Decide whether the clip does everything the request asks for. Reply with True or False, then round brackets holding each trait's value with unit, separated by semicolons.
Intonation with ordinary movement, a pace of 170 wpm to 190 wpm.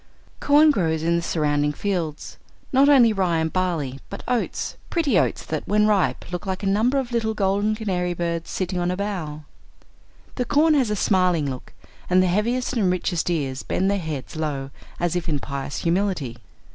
True (4.8 semitones; 185 wpm)